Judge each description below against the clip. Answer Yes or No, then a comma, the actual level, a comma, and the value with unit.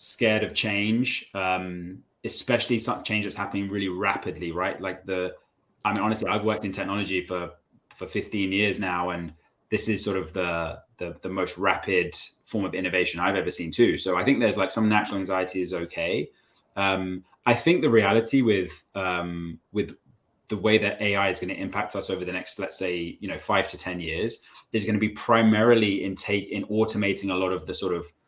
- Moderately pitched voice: No, low, 100 Hz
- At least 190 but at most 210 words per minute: Yes, fast, 205 wpm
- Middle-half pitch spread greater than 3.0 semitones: No, average, 2.7 semitones